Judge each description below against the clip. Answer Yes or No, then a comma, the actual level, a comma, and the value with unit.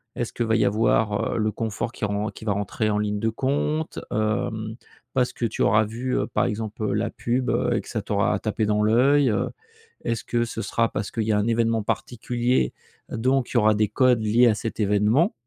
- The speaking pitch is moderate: No, low, 110 Hz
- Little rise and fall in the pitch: Yes, narrow, 2.2 semitones